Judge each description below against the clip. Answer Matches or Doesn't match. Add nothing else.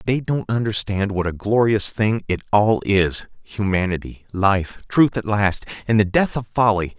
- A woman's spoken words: Doesn't match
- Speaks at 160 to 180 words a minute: Matches